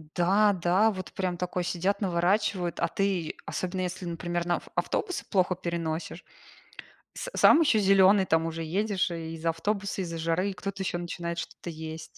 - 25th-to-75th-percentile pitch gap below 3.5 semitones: Yes, narrow, 2.5 semitones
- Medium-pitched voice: Yes, medium, 180 Hz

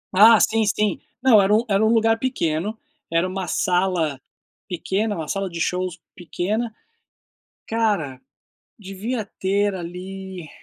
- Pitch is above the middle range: Yes, high, 195 Hz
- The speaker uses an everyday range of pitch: Yes, average, 3.5 semitones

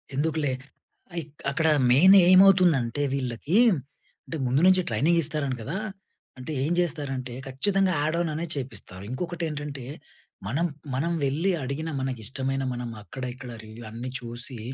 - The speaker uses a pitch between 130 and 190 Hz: Yes, medium, 140 Hz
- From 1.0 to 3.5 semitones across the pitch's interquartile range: No, average, 4.6 semitones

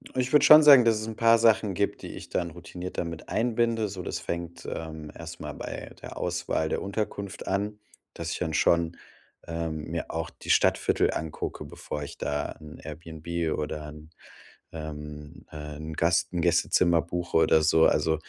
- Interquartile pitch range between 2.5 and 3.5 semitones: No, average, 4.4 semitones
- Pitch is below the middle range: Yes, very low, 85 Hz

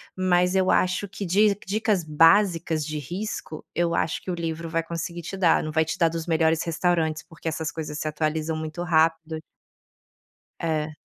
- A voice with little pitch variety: Yes, narrow, 2.0 semitones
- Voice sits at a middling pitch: Yes, medium, 165 Hz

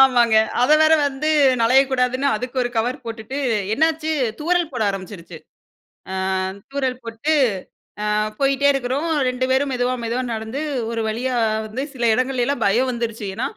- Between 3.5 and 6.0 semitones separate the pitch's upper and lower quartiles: No, average, 3.1 semitones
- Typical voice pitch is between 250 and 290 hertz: Yes, very high, 255 Hz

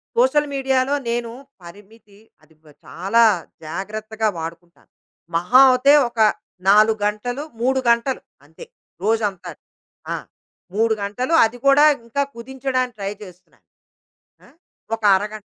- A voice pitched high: Yes, high, 225 Hz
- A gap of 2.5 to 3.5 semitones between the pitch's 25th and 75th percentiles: No, average, 4.2 semitones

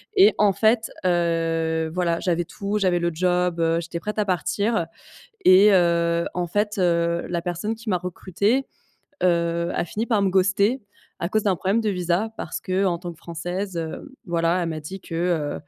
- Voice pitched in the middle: Yes, medium, 180 Hz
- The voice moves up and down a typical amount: Yes, average, 3.0 semitones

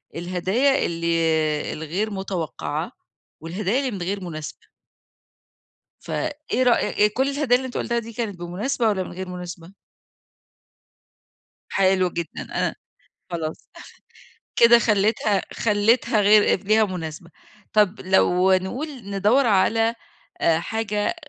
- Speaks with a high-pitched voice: Yes, high, 205 Hz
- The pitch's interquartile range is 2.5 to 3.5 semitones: No, average, 4.3 semitones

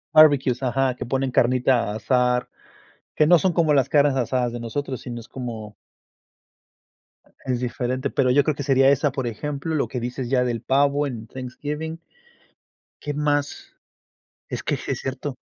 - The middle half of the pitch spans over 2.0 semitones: Yes, average, 2.7 semitones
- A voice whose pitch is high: No, low, 130 Hz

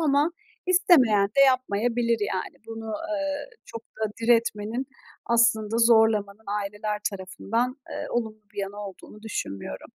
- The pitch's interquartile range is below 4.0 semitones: Yes, average, 2.7 semitones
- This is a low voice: No, high, 225 Hz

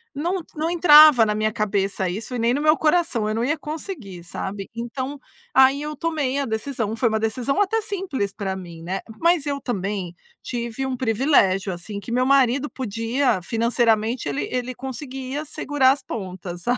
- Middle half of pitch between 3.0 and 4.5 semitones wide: No, average, 5.2 semitones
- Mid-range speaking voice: No, high, 245 Hz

